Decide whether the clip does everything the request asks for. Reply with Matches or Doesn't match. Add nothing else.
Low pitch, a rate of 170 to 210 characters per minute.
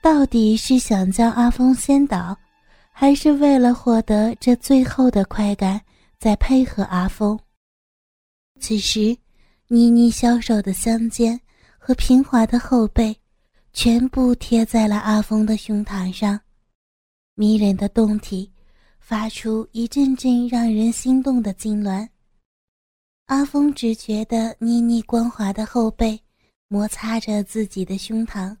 Doesn't match